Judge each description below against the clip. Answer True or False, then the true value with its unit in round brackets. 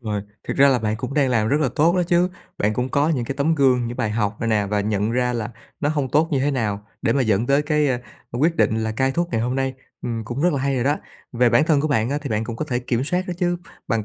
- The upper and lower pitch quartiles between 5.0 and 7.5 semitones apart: False (4.5 semitones)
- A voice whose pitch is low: True (130 Hz)